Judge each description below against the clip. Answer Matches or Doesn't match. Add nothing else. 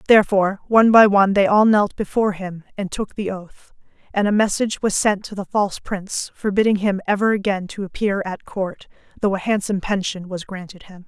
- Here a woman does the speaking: Matches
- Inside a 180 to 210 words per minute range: Matches